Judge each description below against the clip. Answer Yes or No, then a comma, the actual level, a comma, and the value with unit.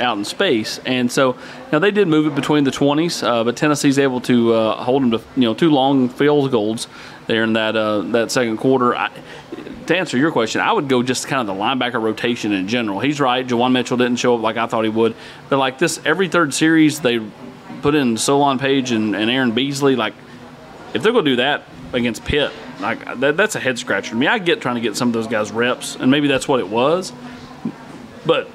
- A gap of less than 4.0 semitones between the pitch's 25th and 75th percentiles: Yes, average, 3.4 semitones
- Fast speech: Yes, fast, 230 wpm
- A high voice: No, low, 125 Hz